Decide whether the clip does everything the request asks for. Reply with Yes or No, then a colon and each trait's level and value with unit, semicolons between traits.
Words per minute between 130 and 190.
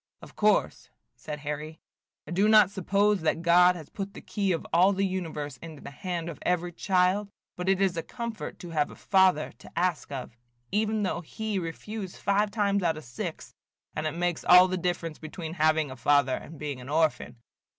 No: average, 200 wpm